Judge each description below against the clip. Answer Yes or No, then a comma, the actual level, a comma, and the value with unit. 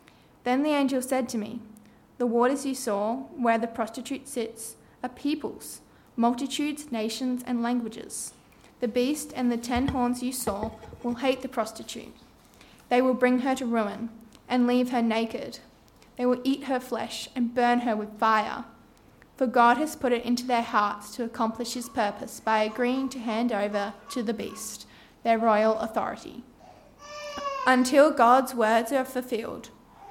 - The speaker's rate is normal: Yes, average, 160 wpm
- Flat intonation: Yes, narrow, 2.3 semitones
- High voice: Yes, high, 245 Hz